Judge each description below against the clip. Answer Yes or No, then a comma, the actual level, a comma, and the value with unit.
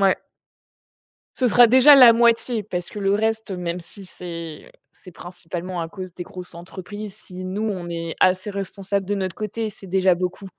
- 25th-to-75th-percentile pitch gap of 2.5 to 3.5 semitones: Yes, average, 2.9 semitones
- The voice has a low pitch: No, high, 190 Hz